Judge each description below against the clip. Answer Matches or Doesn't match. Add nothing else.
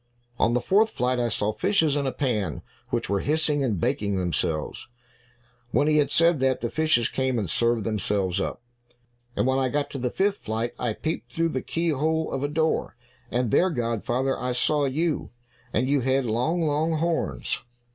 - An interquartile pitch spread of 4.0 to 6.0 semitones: Matches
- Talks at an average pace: Matches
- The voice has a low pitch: Matches